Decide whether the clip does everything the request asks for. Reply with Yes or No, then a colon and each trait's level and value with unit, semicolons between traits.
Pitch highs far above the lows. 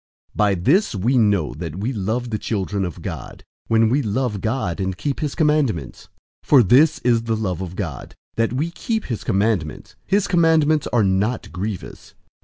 Yes: wide, 6.0 semitones